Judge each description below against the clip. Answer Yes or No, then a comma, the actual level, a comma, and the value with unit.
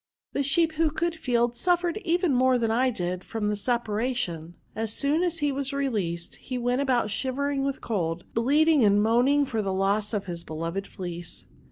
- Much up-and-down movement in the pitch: Yes, wide, 5.7 semitones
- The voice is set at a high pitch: Yes, high, 245 Hz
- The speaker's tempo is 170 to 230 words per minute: Yes, average, 195 wpm